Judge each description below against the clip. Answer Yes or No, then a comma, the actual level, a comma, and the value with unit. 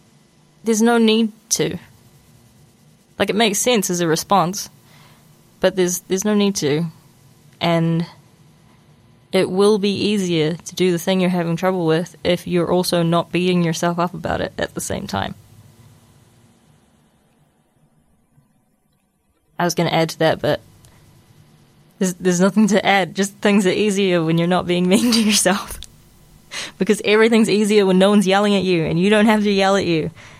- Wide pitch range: No, average, 3.5 semitones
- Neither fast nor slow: Yes, average, 165 wpm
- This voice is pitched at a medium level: Yes, medium, 180 Hz